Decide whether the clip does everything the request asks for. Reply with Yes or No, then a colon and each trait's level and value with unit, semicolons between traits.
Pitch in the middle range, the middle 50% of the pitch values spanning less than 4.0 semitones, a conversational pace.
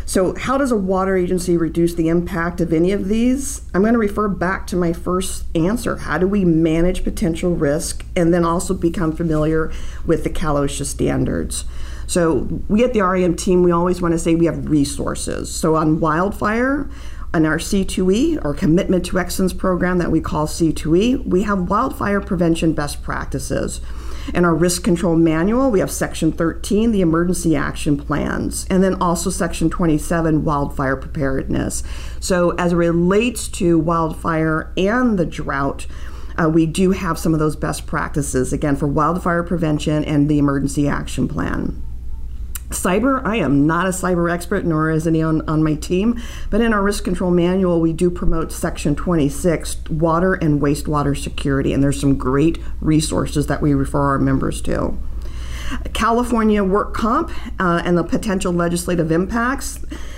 Yes: medium, 170 Hz; average, 3.6 semitones; average, 165 wpm